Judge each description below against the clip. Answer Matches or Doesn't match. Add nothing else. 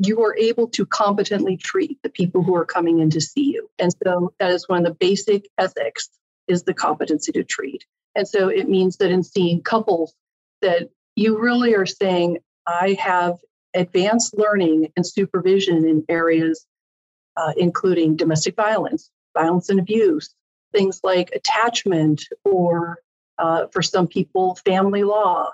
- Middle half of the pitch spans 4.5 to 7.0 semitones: Doesn't match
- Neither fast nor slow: Matches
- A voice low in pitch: Doesn't match